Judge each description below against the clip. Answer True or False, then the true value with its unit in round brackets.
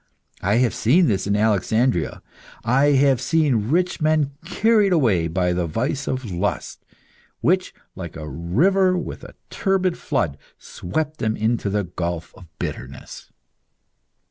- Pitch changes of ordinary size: False (8.9 semitones)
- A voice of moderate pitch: False (120 Hz)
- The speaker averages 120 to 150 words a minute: True (140 wpm)